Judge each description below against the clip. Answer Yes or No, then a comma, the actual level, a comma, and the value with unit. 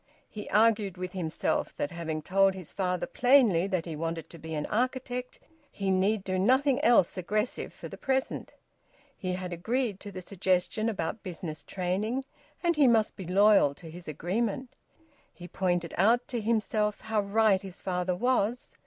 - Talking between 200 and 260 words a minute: No, average, 170 wpm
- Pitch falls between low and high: No, high, 195 Hz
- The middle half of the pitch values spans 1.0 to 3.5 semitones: No, average, 4.2 semitones